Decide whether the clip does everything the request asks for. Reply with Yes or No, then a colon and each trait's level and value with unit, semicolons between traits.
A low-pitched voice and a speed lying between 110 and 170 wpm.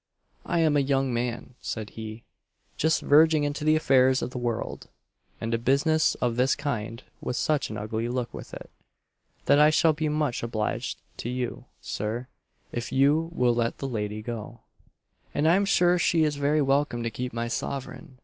No: low, 130 Hz; average, 185 wpm